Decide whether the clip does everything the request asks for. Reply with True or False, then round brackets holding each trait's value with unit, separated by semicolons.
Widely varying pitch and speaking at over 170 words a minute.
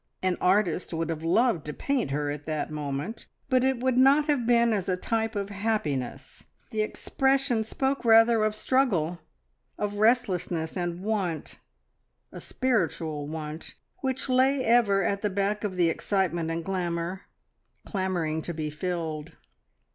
False (6.0 semitones; 150 wpm)